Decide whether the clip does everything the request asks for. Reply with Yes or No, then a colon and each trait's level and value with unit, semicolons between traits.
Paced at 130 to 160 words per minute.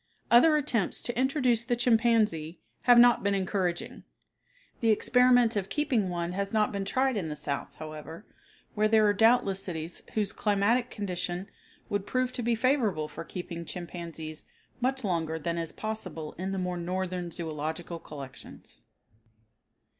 Yes: average, 150 wpm